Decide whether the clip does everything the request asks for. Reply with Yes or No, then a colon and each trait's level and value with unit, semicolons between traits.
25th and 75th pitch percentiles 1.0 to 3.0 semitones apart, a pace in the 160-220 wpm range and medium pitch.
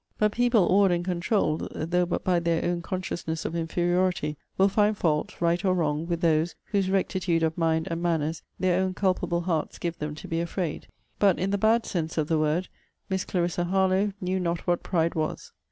Yes: narrow, 2.4 semitones; average, 200 wpm; medium, 175 Hz